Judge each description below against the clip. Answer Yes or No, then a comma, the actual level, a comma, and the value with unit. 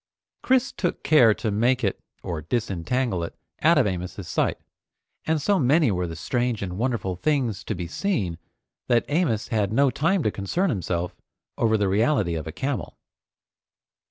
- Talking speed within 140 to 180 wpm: Yes, average, 165 wpm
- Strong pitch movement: Yes, wide, 7.2 semitones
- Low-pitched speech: Yes, low, 115 Hz